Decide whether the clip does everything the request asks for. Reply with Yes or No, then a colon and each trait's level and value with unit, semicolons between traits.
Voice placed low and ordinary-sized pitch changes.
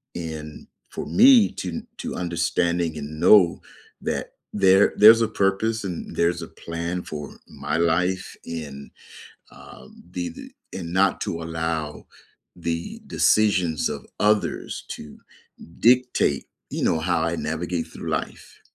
Yes: very low, 85 Hz; average, 3.1 semitones